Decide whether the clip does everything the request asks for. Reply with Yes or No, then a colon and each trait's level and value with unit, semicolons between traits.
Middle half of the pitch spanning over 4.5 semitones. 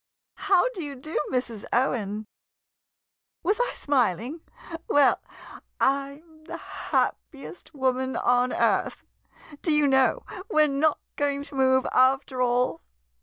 No: average, 3.1 semitones